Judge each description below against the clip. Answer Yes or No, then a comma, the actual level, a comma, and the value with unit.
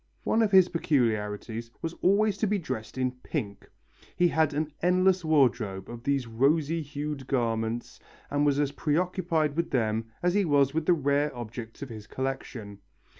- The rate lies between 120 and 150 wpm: No, average, 170 wpm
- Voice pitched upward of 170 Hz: No, medium, 140 Hz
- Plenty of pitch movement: Yes, wide, 5.8 semitones